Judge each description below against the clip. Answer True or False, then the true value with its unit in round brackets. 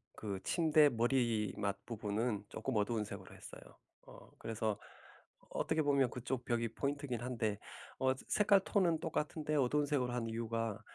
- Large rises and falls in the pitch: False (4.5 semitones)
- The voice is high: False (120 Hz)